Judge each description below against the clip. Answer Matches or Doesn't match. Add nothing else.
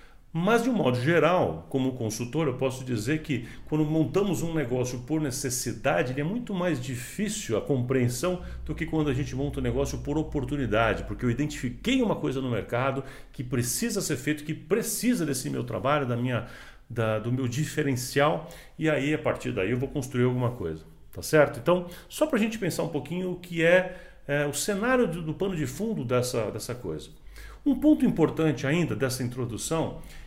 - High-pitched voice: Doesn't match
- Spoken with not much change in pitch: Doesn't match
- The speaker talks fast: Matches